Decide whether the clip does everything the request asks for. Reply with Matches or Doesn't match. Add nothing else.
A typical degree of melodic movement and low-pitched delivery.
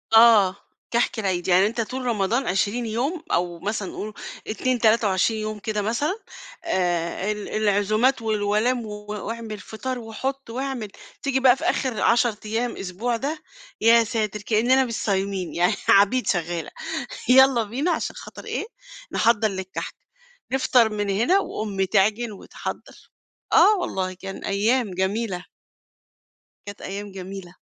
Doesn't match